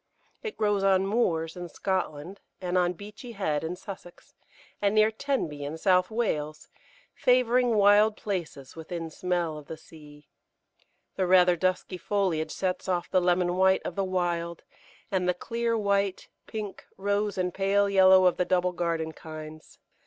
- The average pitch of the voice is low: No, medium, 185 Hz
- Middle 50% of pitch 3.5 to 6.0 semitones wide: No, average, 3.1 semitones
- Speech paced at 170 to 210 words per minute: No, average, 155 wpm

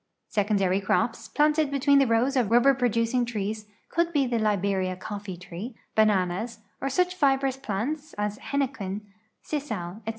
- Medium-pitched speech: No, high, 230 Hz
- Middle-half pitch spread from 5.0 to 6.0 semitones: Yes, average, 5.3 semitones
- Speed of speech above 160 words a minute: No, average, 155 wpm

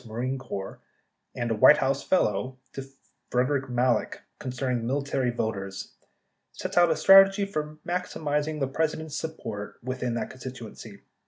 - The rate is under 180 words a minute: Yes, average, 145 wpm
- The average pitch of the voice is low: Yes, low, 130 Hz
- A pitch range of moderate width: Yes, average, 4.2 semitones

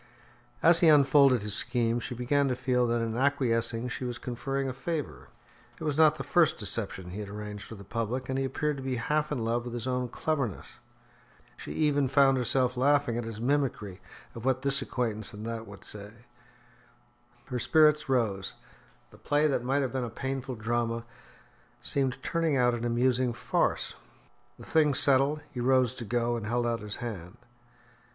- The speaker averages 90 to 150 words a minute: No, average, 185 wpm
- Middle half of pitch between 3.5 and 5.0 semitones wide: No, average, 3.0 semitones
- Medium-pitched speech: No, low, 125 Hz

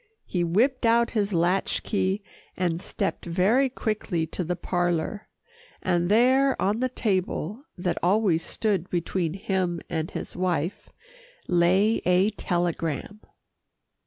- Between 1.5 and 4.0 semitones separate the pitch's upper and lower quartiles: Yes, average, 3.7 semitones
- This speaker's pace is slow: Yes, slow, 125 wpm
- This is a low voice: No, medium, 185 Hz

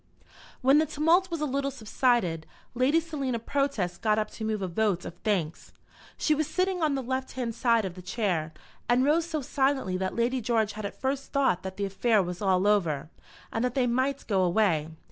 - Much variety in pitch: Yes, wide, 6.3 semitones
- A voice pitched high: Yes, high, 235 Hz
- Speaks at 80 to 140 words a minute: No, fast, 205 wpm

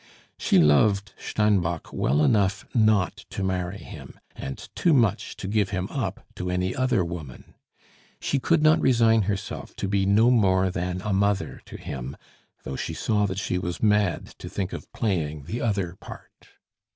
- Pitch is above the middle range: No, low, 100 Hz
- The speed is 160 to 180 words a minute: Yes, average, 170 wpm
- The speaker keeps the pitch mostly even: No, average, 3.0 semitones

